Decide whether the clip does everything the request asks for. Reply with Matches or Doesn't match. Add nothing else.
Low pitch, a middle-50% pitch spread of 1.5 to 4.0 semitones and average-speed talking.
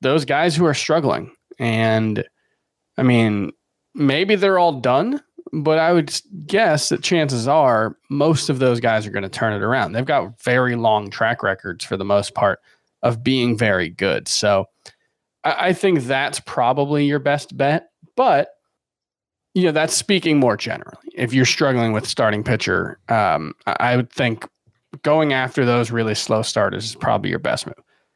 Doesn't match